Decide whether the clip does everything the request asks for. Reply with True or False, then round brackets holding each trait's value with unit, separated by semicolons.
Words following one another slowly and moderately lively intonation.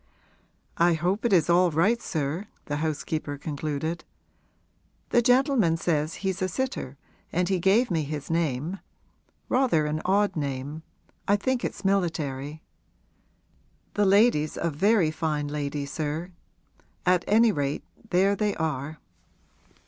True (130 wpm; 4.8 semitones)